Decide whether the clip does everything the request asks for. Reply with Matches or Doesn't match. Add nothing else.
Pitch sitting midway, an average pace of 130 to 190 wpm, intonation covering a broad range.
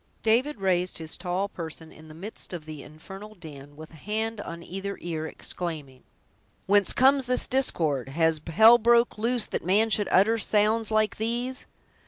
Doesn't match